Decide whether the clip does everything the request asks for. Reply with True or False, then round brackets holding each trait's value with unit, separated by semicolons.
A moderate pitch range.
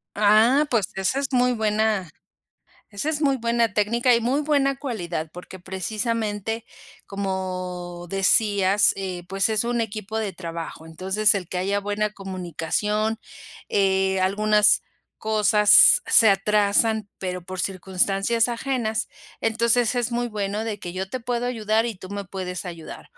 True (3.3 semitones)